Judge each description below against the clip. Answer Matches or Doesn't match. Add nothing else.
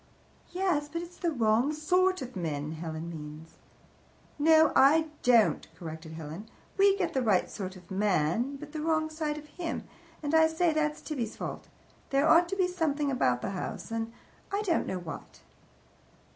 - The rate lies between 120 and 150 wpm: Doesn't match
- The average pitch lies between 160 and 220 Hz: Doesn't match